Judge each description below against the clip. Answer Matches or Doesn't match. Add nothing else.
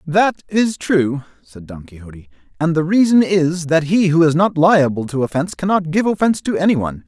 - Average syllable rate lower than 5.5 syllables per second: Matches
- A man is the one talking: Matches